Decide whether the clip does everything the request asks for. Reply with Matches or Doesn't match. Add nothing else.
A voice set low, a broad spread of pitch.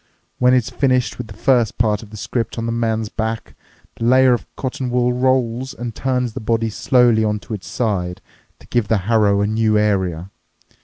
Doesn't match